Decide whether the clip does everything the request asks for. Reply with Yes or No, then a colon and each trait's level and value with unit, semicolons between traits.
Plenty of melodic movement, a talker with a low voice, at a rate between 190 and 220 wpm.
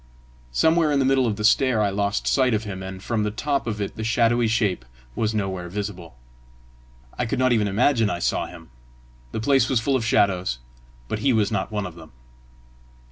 No: average, 4.0 semitones; low, 110 Hz; fast, 205 wpm